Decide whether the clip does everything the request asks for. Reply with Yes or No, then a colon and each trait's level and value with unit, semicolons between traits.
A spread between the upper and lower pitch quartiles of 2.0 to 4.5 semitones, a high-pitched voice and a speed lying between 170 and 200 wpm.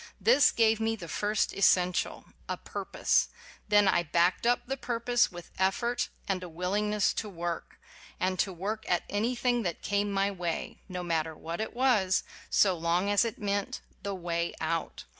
Yes: average, 3.9 semitones; high, 195 Hz; average, 175 wpm